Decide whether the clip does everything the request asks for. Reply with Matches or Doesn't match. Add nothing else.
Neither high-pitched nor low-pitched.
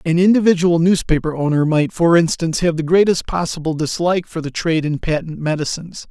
Matches